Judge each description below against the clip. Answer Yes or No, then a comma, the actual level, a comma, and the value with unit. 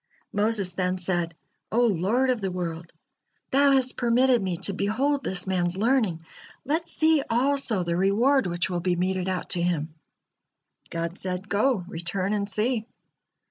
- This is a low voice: No, high, 195 Hz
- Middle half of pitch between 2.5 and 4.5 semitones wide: No, wide, 5.5 semitones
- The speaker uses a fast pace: No, average, 155 wpm